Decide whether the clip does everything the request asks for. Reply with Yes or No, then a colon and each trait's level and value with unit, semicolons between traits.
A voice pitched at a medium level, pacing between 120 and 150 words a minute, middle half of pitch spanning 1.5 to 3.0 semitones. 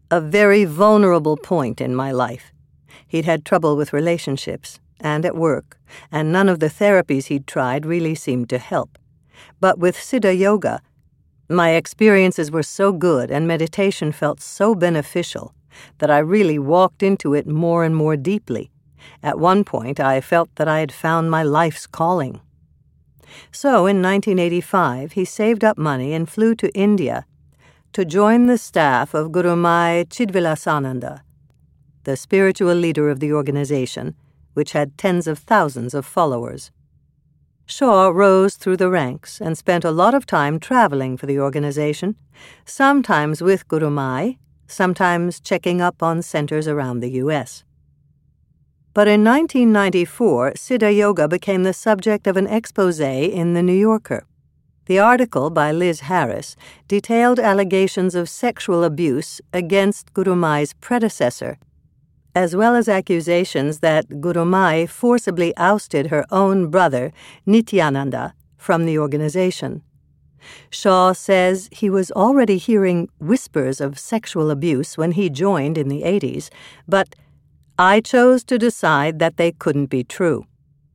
No: medium, 175 Hz; average, 140 wpm; average, 4.6 semitones